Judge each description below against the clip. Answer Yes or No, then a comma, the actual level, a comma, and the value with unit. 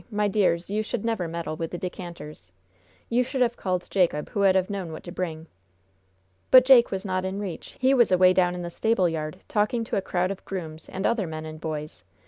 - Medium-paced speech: No, fast, 225 wpm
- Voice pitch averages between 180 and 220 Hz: Yes, medium, 185 Hz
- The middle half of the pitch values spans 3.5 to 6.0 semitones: Yes, average, 3.9 semitones